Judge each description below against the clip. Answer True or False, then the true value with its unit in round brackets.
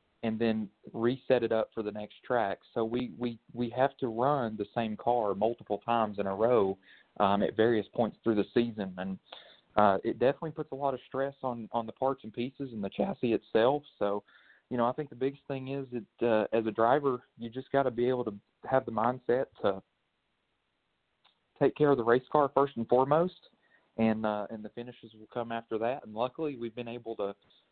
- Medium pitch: False (120 Hz)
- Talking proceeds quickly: True (215 wpm)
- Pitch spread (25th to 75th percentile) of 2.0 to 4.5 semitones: True (3.1 semitones)